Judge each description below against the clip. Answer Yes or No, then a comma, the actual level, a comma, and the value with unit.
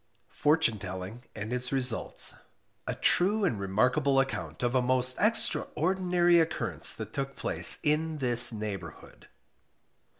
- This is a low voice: Yes, low, 130 Hz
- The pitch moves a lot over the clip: Yes, wide, 6.3 semitones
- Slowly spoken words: Yes, slow, 125 wpm